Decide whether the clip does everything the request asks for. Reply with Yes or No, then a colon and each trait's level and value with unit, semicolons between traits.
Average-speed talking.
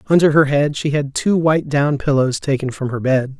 No: fast, 230 wpm